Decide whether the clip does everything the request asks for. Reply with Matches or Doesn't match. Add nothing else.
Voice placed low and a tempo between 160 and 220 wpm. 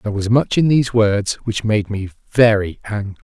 Matches